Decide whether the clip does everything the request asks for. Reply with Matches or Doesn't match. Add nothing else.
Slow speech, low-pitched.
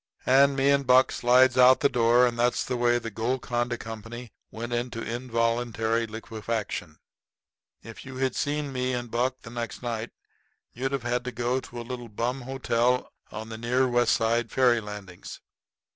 Doesn't match